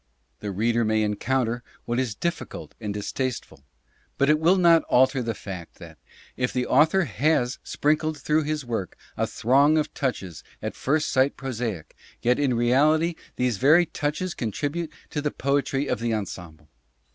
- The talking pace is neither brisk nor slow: Yes, average, 160 wpm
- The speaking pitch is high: No, low, 130 Hz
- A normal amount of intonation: Yes, average, 4.9 semitones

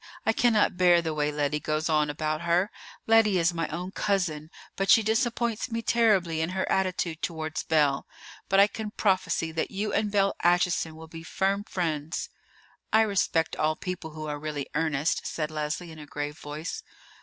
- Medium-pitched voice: Yes, medium, 170 Hz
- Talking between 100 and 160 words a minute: No, average, 180 wpm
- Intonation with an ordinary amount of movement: Yes, average, 4.2 semitones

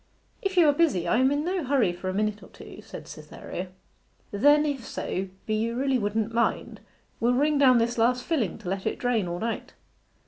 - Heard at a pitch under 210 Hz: No, high, 240 Hz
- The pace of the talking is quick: Yes, fast, 210 wpm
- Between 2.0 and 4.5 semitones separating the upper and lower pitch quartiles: No, average, 5.1 semitones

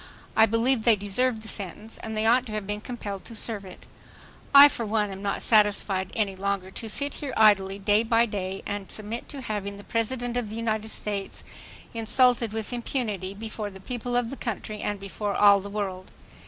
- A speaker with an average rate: Yes, average, 195 wpm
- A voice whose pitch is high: Yes, high, 215 Hz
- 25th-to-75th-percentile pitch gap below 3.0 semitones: Yes, narrow, 2.6 semitones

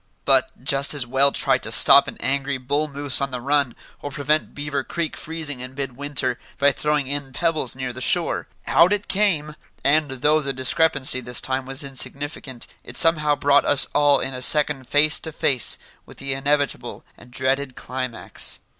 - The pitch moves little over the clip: Yes, narrow, 2.2 semitones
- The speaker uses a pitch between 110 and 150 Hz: Yes, medium, 140 Hz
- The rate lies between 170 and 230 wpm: Yes, average, 180 wpm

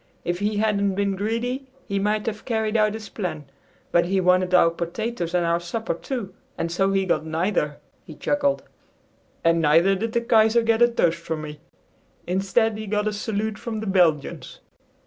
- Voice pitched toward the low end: No, high, 200 Hz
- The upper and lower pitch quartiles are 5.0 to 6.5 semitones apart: No, average, 4.2 semitones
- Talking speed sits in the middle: Yes, average, 185 wpm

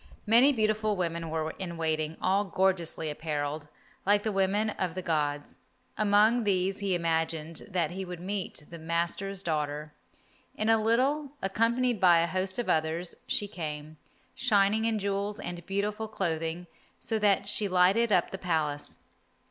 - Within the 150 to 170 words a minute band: Yes, average, 155 wpm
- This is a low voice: No, medium, 185 Hz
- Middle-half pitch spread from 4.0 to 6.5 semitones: Yes, average, 4.3 semitones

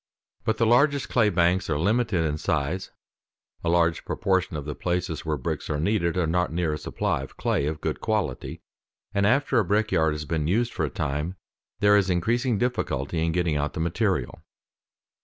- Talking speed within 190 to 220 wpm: Yes, average, 195 wpm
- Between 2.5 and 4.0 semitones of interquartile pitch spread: No, average, 5.2 semitones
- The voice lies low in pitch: Yes, very low, 85 Hz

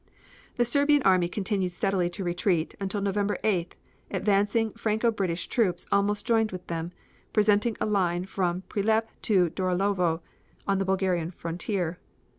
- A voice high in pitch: Yes, high, 195 Hz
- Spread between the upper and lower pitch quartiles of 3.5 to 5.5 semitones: No, average, 2.9 semitones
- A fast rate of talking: No, average, 145 wpm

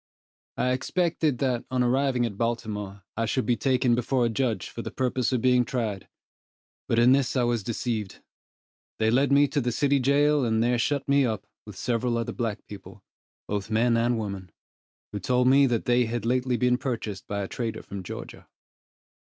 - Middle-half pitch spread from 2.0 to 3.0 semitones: Yes, narrow, 2.5 semitones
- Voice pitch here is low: Yes, low, 120 Hz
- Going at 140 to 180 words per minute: No, average, 190 wpm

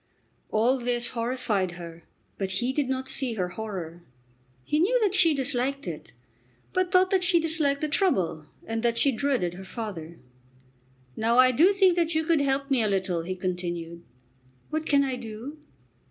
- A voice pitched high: Yes, very high, 250 Hz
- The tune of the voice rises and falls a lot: Yes, wide, 7.9 semitones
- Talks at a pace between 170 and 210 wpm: Yes, average, 175 wpm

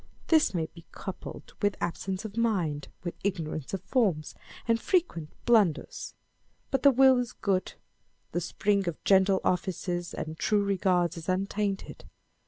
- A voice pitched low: No, high, 190 Hz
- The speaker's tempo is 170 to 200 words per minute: No, average, 150 wpm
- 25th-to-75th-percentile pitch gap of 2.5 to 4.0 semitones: Yes, average, 3.6 semitones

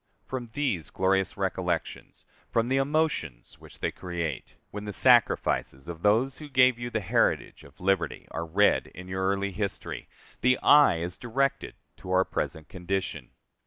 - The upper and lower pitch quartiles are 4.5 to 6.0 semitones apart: Yes, wide, 5.6 semitones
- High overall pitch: No, very low, 95 Hz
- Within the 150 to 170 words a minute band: Yes, average, 160 wpm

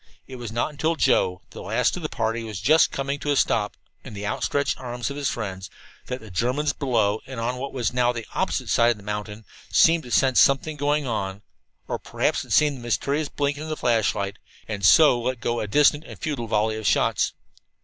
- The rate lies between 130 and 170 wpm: No, fast, 205 wpm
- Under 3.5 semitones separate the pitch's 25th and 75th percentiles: No, average, 4.6 semitones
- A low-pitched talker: Yes, low, 125 Hz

